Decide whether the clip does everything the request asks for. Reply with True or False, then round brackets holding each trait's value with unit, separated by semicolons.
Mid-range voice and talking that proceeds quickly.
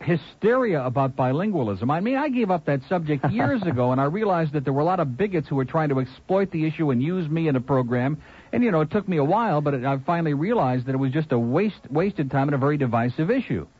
True (150 Hz; 260 wpm)